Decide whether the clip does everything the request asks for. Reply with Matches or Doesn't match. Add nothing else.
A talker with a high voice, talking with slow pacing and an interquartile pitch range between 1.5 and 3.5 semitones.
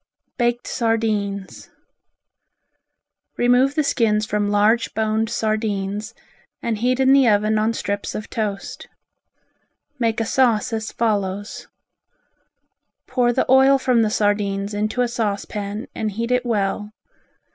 Matches